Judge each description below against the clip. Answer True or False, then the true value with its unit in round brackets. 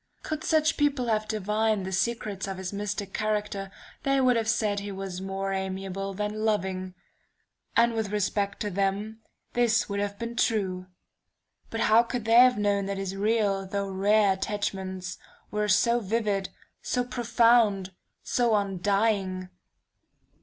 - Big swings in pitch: False (2.6 semitones)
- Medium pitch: False (205 Hz)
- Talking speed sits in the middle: True (145 wpm)